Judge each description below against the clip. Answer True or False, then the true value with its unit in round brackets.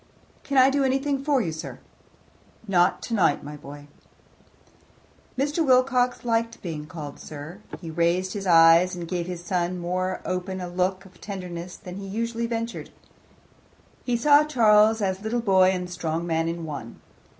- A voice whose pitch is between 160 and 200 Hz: True (185 Hz)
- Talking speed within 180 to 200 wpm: False (160 wpm)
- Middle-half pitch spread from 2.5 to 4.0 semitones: False (5.2 semitones)